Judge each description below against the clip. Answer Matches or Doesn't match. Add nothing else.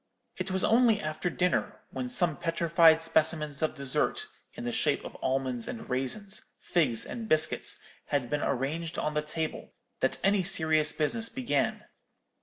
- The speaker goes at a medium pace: Matches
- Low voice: Doesn't match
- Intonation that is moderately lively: Matches